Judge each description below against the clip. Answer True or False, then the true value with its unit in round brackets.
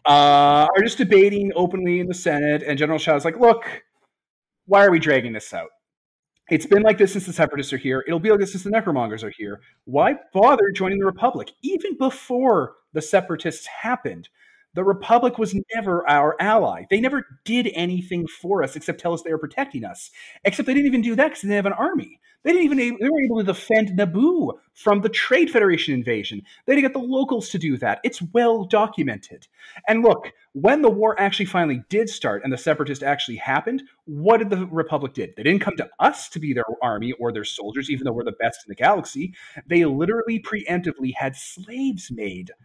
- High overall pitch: True (195 Hz)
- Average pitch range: False (7.0 semitones)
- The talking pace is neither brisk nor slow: False (210 wpm)